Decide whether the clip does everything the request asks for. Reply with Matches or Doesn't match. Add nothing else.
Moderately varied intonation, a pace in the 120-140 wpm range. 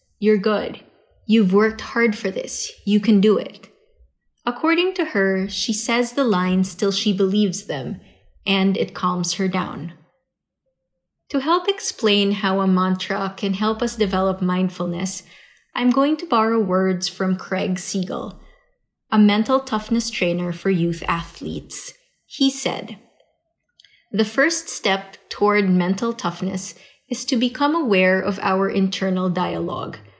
Matches